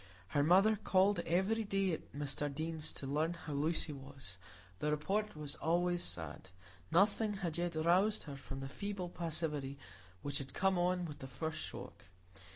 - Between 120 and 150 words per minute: No, average, 160 wpm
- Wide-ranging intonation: No, average, 4.5 semitones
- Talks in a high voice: No, medium, 160 Hz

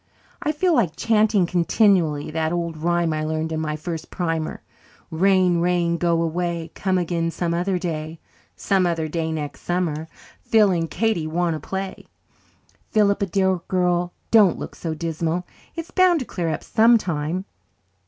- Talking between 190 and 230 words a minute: No, average, 155 wpm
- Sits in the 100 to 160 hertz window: No, medium, 175 Hz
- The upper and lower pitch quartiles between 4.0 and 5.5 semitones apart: No, average, 2.9 semitones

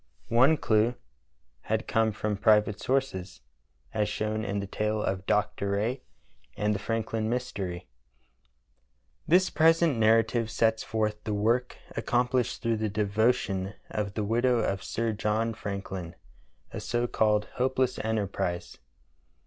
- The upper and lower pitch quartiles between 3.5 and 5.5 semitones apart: No, narrow, 2.4 semitones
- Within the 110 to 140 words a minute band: Yes, slow, 135 wpm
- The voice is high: No, low, 110 Hz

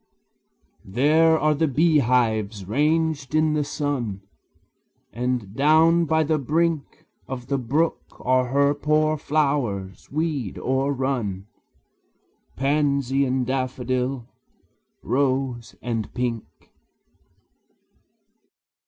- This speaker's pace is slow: Yes, slow, 90 wpm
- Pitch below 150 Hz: Yes, low, 135 Hz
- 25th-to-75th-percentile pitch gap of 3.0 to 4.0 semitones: Yes, average, 3.7 semitones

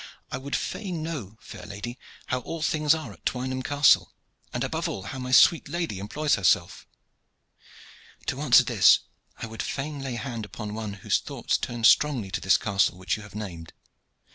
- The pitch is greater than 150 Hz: No, low, 120 Hz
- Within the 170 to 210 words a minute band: Yes, average, 180 wpm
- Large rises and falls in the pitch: Yes, wide, 5.8 semitones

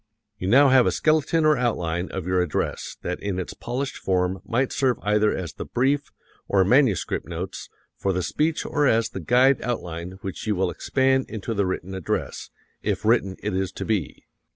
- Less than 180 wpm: No, average, 190 wpm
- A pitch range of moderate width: No, wide, 5.8 semitones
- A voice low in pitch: Yes, low, 105 Hz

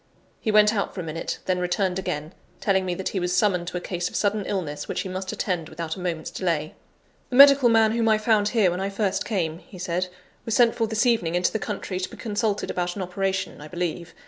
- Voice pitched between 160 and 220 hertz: Yes, high, 190 Hz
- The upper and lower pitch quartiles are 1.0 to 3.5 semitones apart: Yes, average, 3.2 semitones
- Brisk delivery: Yes, fast, 245 wpm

